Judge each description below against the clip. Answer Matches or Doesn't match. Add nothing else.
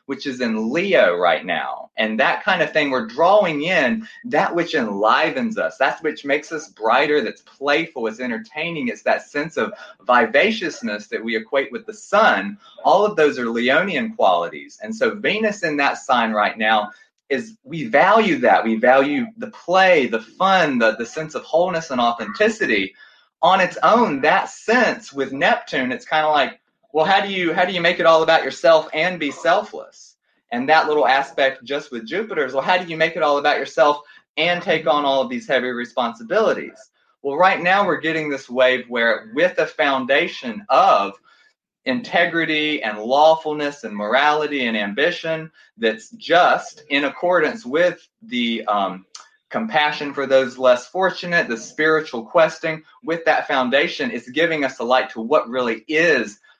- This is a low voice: Doesn't match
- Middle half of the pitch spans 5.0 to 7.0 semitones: Matches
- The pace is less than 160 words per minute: Doesn't match